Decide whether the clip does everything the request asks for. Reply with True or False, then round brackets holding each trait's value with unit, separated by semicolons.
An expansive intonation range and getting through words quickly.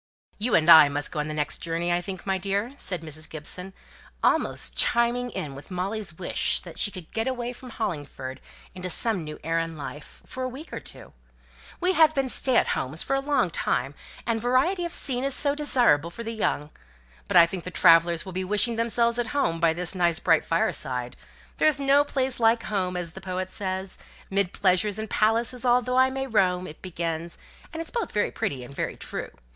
True (6.7 semitones; 210 wpm)